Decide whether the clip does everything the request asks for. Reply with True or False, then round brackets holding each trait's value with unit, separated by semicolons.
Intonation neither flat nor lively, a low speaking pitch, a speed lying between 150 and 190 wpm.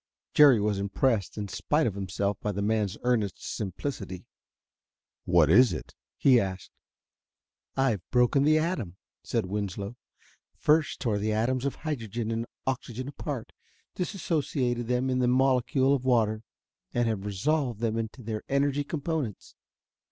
False (4.7 semitones; 120 Hz; 140 wpm)